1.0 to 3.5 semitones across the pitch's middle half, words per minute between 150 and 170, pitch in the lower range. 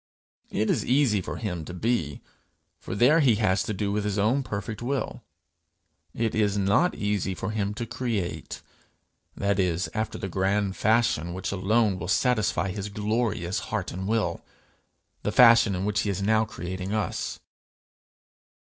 Yes: average, 2.7 semitones; average, 160 wpm; low, 105 Hz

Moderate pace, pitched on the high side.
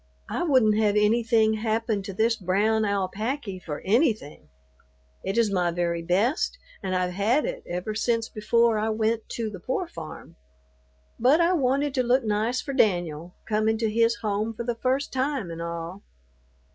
Yes: average, 170 wpm; high, 220 Hz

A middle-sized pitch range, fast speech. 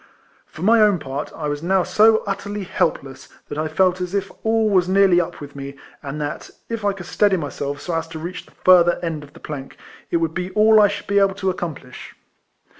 Yes: average, 4.7 semitones; fast, 225 wpm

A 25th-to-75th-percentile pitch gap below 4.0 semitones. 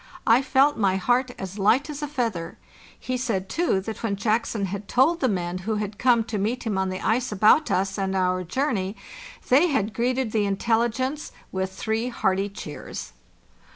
No: average, 4.7 semitones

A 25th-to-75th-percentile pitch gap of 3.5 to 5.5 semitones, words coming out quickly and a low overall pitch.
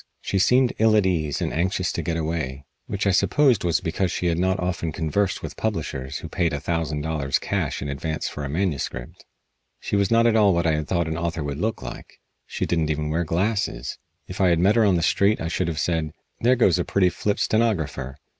Yes: average, 4.1 semitones; fast, 230 wpm; very low, 85 Hz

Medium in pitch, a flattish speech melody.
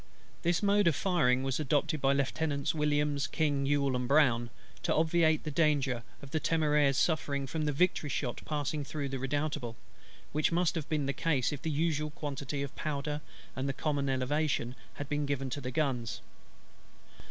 Yes: medium, 145 Hz; narrow, 2.3 semitones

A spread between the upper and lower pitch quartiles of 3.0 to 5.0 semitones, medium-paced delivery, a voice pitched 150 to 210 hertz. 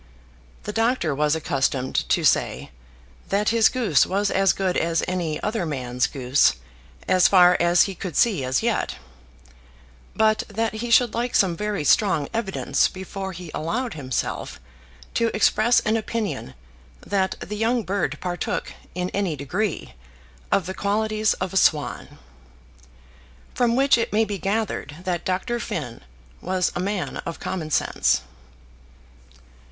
Yes: average, 4.7 semitones; average, 145 wpm; high, 190 Hz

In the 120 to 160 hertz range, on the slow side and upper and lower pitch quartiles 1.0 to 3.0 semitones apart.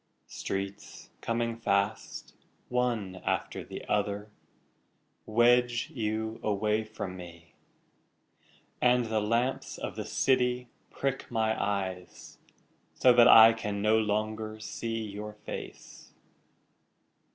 No: low, 110 Hz; slow, 105 wpm; narrow, 2.4 semitones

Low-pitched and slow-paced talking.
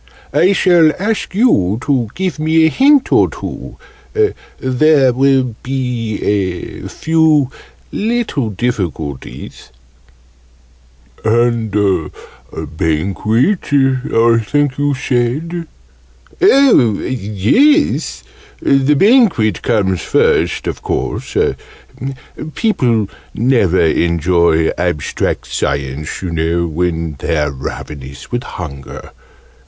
Yes: low, 115 Hz; slow, 90 wpm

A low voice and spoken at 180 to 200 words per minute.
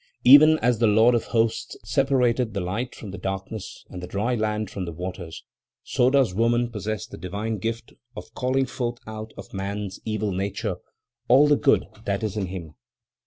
Yes: low, 110 Hz; average, 185 wpm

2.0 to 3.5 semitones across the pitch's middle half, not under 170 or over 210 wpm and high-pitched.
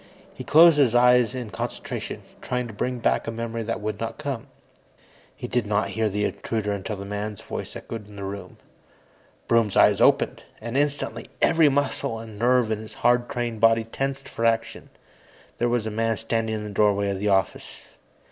No: average, 2.7 semitones; average, 190 wpm; low, 115 Hz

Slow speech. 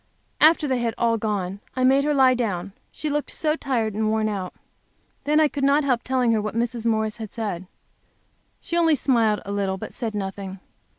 No: average, 200 wpm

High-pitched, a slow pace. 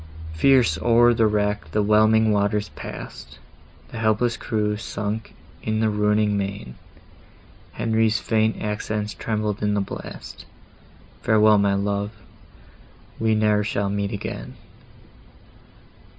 No: low, 105 Hz; slow, 110 wpm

